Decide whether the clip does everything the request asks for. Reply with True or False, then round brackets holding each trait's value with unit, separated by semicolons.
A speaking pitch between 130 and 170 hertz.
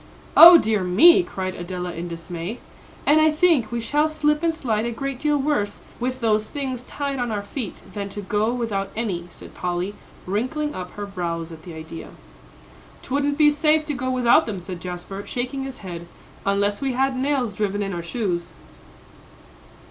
False (220 Hz)